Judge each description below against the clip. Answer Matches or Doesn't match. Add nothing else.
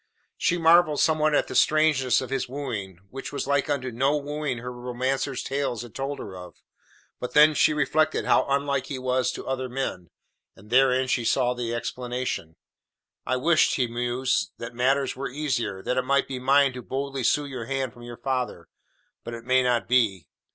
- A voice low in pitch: Matches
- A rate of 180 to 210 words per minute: Matches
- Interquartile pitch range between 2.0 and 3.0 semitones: Matches